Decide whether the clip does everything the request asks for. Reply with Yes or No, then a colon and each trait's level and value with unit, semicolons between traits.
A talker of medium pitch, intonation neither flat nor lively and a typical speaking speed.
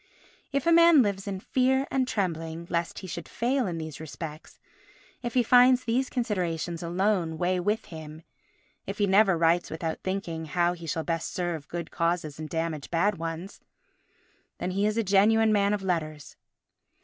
Yes: medium, 180 Hz; average, 4.5 semitones; average, 175 wpm